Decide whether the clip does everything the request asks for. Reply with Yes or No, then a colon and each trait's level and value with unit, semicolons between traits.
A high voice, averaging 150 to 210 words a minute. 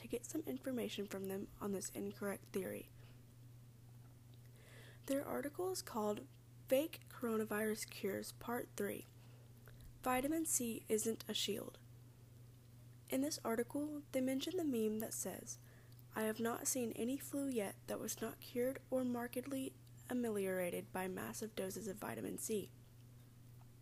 No: high, 200 Hz; slow, 135 wpm